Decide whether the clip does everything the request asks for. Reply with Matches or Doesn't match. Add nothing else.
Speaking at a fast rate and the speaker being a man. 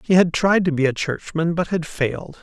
Matches